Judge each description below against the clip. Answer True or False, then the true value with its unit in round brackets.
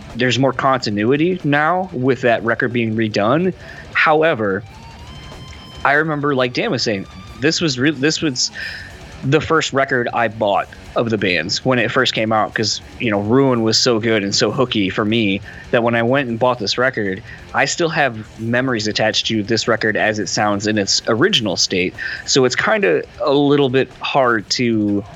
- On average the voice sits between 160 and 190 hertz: False (120 Hz)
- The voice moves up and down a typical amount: True (3.7 semitones)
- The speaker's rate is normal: True (185 wpm)